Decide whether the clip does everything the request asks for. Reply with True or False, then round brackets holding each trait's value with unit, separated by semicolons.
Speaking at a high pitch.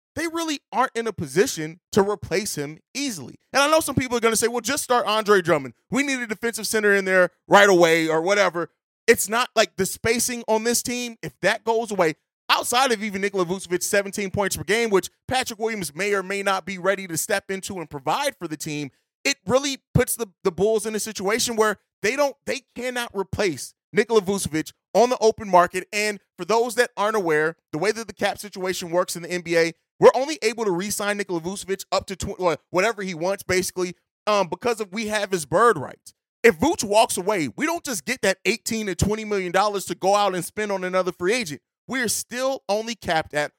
True (205 Hz)